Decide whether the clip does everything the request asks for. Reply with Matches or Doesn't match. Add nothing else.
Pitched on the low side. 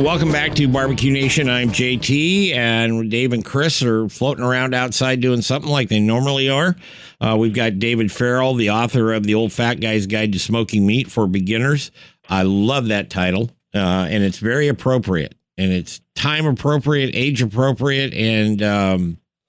Matches